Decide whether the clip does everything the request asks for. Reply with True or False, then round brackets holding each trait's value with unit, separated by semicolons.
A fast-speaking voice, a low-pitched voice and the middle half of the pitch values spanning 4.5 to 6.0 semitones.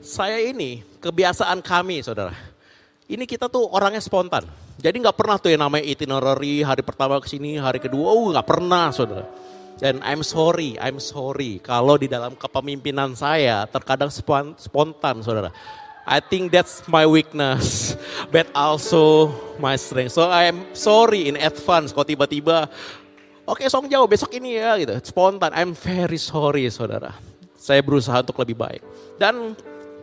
False (150 wpm; 145 Hz; 4.8 semitones)